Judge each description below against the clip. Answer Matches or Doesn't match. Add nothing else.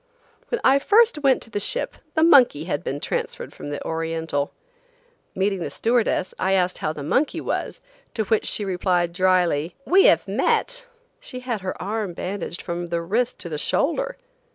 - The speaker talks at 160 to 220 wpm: Matches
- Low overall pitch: Doesn't match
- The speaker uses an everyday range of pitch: Doesn't match